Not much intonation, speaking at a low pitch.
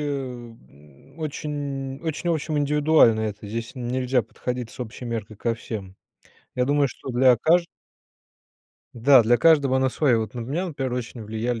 No: average, 3.8 semitones; low, 125 Hz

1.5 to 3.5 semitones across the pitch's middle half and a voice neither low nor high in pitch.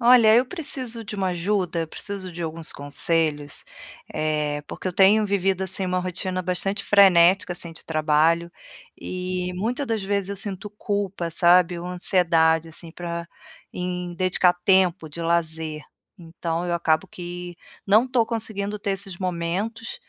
Yes: average, 3.0 semitones; medium, 180 Hz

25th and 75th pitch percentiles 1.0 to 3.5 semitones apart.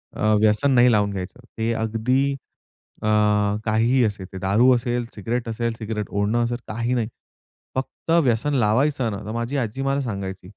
Yes: average, 2.8 semitones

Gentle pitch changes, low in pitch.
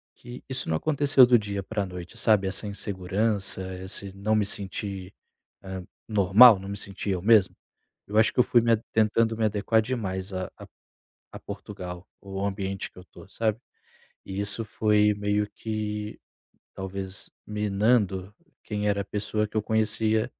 Yes: narrow, 2.2 semitones; low, 105 Hz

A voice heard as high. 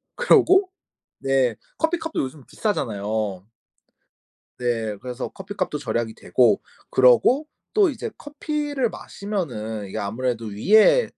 No: low, 135 Hz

